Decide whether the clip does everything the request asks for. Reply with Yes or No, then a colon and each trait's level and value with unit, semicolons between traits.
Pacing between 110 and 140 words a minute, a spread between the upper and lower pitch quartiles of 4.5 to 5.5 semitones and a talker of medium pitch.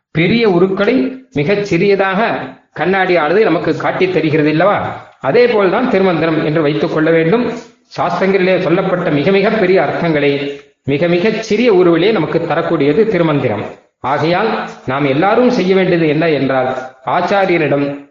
Yes: average, 125 wpm; average, 5.1 semitones; medium, 175 Hz